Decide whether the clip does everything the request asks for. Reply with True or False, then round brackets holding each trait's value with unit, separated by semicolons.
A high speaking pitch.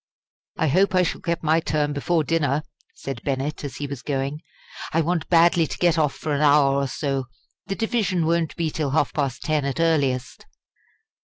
False (155 Hz)